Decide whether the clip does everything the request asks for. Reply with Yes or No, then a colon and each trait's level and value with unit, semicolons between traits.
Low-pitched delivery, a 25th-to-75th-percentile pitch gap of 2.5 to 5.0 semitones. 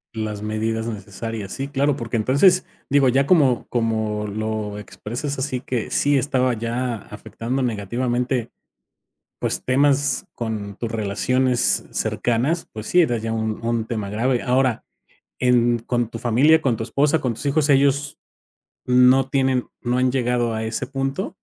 Yes: low, 125 Hz; average, 3.2 semitones